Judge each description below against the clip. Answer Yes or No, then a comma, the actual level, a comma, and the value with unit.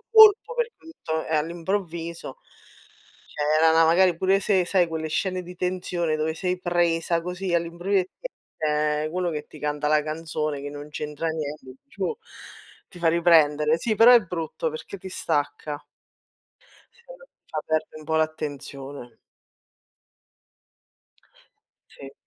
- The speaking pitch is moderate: Yes, medium, 165 Hz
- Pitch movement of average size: Yes, average, 3.2 semitones